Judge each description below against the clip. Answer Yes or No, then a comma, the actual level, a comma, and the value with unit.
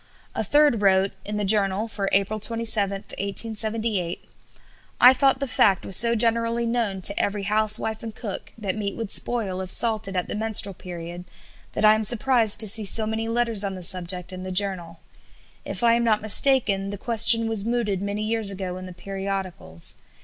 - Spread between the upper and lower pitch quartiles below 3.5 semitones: Yes, average, 2.8 semitones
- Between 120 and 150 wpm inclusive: No, average, 185 wpm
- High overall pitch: Yes, high, 210 Hz